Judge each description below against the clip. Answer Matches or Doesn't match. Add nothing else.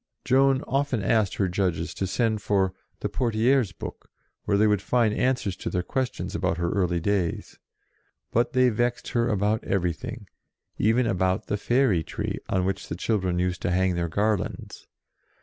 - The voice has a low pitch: Matches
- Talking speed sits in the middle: Matches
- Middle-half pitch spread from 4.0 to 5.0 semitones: Matches